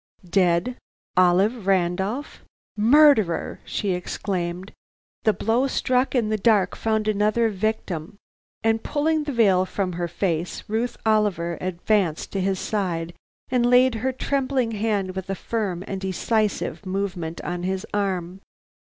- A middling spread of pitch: Yes, average, 3.7 semitones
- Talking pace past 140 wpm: No, slow, 135 wpm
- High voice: Yes, high, 200 Hz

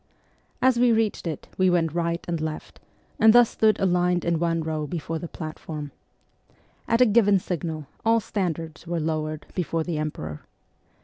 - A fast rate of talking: No, average, 165 wpm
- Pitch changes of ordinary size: Yes, average, 3.9 semitones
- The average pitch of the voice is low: No, medium, 170 Hz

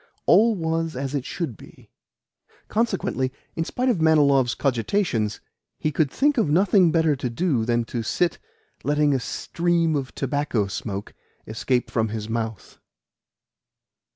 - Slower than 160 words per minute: Yes, average, 140 wpm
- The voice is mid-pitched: Yes, medium, 145 Hz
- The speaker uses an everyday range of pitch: No, wide, 6.0 semitones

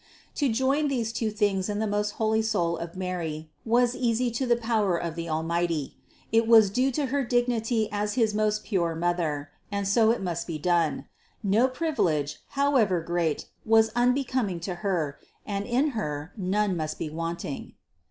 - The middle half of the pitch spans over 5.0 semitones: Yes, wide, 5.5 semitones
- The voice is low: No, high, 205 Hz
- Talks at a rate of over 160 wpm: Yes, average, 170 wpm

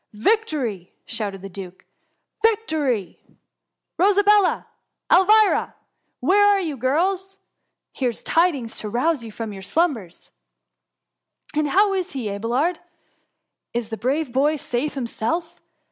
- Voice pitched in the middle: No, very high, 280 Hz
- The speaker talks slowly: Yes, slow, 130 wpm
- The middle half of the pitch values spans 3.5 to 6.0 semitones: No, wide, 8.5 semitones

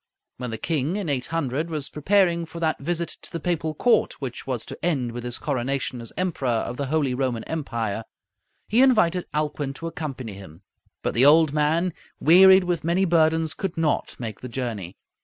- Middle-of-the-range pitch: Yes, medium, 150 Hz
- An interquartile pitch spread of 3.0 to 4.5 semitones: No, average, 5.1 semitones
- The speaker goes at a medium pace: Yes, average, 185 wpm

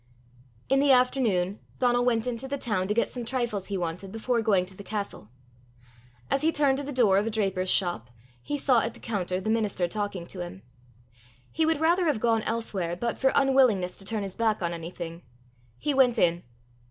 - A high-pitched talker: Yes, high, 220 Hz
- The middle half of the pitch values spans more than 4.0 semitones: Yes, wide, 5.4 semitones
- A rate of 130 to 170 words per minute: No, fast, 205 wpm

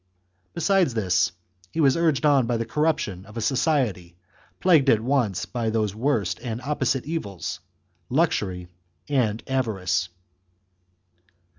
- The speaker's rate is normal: No, slow, 130 wpm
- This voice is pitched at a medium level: No, low, 120 Hz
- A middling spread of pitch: No, wide, 5.7 semitones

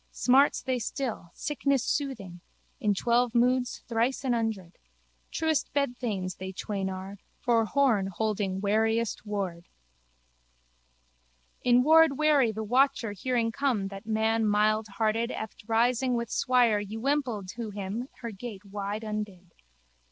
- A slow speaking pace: Yes, slow, 125 wpm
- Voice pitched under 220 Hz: No, high, 225 Hz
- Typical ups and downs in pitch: Yes, average, 3.6 semitones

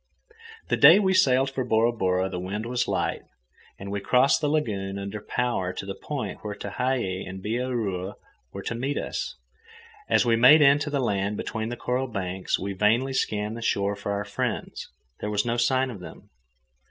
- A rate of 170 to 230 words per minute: Yes, average, 190 wpm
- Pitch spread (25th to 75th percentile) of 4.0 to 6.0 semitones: Yes, average, 4.5 semitones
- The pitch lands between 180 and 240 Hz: No, low, 110 Hz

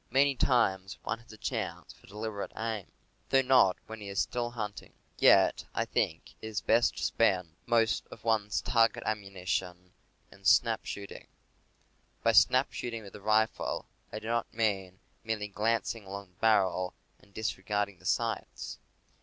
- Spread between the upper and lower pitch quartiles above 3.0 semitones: No, average, 2.7 semitones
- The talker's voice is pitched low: Yes, low, 110 Hz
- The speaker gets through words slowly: No, average, 165 wpm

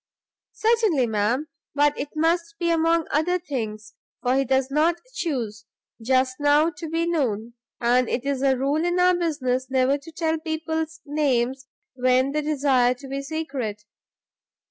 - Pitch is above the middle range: Yes, very high, 280 Hz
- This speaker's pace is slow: No, average, 155 wpm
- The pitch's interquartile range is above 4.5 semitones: No, average, 3.9 semitones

